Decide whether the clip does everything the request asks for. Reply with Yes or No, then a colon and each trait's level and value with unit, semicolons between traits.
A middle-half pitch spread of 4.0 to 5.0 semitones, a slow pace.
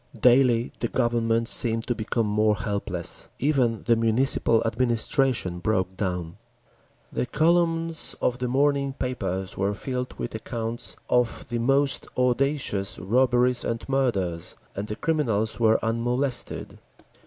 No: average, 3.1 semitones; slow, 125 wpm